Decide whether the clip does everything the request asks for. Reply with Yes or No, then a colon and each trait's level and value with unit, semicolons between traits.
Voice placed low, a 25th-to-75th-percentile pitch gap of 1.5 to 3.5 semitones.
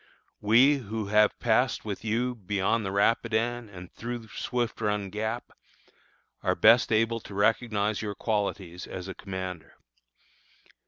Yes: low, 110 Hz; narrow, 2.4 semitones